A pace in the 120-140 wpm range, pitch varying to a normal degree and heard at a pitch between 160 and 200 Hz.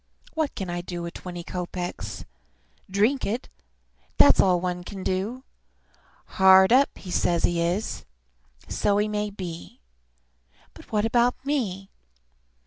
Yes: slow, 135 wpm; average, 3.6 semitones; high, 190 Hz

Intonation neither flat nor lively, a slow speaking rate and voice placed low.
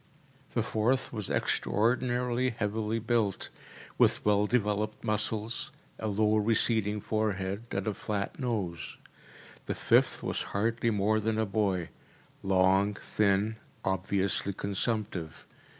No: narrow, 2.2 semitones; slow, 115 wpm; low, 105 Hz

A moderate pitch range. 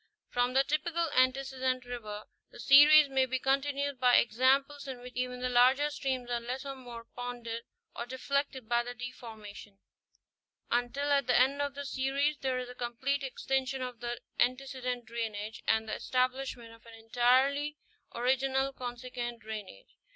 No: narrow, 2.1 semitones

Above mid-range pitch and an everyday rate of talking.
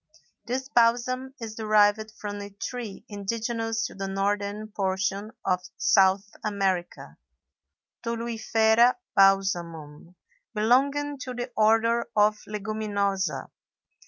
No: high, 215 Hz; slow, 100 wpm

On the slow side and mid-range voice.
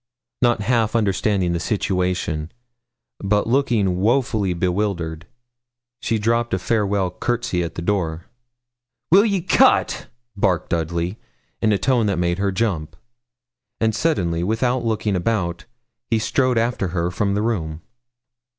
No: slow, 130 wpm; low, 100 Hz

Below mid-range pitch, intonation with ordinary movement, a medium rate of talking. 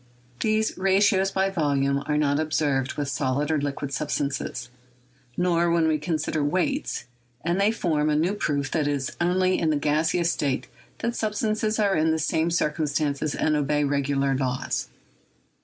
No: medium, 155 Hz; average, 4.0 semitones; average, 170 wpm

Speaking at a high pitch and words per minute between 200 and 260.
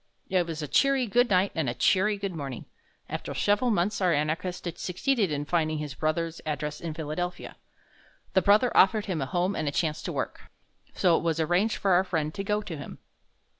No: medium, 175 Hz; fast, 205 wpm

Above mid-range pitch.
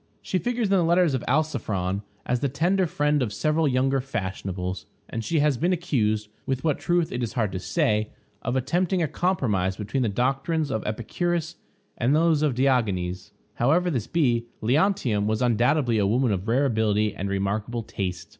No: low, 125 Hz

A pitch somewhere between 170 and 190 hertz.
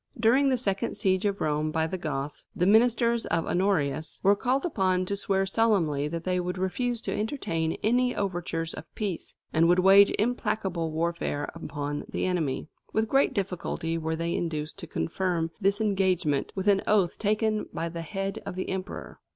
Yes: medium, 185 Hz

